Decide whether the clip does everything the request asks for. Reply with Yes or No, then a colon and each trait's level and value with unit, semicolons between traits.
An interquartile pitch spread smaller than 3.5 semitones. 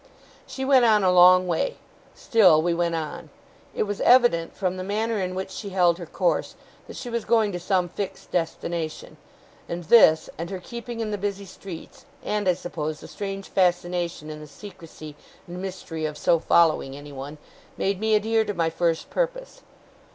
No: average, 3.8 semitones